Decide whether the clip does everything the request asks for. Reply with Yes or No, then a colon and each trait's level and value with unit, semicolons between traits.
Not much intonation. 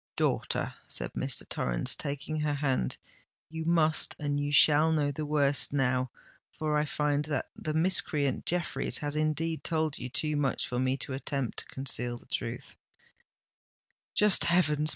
Yes: narrow, 2.2 semitones